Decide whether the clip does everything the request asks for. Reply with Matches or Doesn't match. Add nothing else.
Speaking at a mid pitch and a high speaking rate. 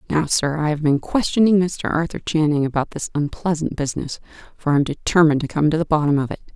Matches